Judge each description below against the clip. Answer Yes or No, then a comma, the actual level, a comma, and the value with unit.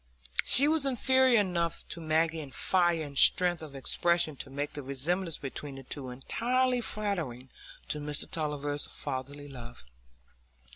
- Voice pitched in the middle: Yes, medium, 155 Hz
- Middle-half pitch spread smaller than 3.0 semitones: No, average, 4.6 semitones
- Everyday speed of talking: Yes, average, 145 wpm